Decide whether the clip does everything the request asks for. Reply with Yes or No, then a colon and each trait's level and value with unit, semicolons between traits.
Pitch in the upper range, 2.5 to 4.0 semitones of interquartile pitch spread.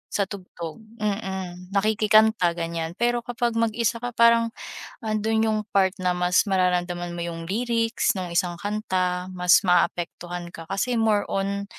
Yes: high, 195 Hz; average, 3.7 semitones